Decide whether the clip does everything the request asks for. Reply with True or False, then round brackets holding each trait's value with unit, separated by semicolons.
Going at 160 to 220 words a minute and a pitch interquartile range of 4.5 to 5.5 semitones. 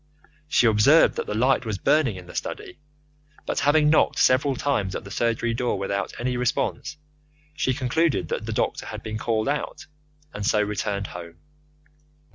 True (165 wpm; 5.0 semitones)